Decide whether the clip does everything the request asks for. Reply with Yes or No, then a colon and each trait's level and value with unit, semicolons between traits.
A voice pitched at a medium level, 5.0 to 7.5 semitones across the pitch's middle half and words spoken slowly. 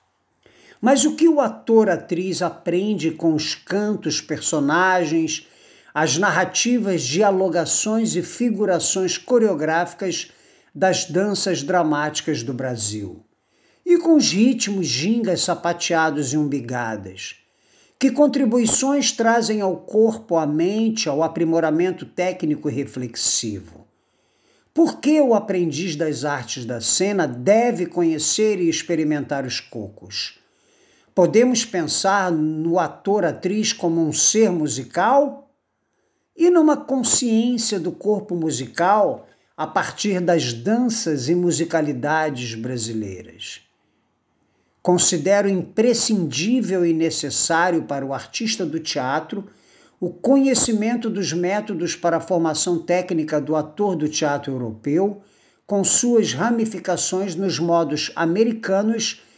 Yes: medium, 180 Hz; wide, 5.6 semitones; slow, 105 wpm